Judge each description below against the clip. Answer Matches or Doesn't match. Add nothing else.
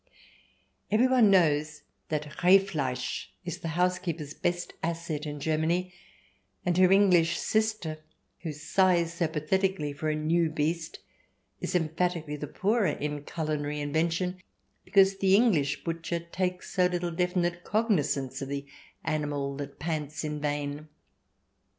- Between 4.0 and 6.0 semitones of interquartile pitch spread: Doesn't match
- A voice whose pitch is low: Doesn't match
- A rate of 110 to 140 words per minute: Matches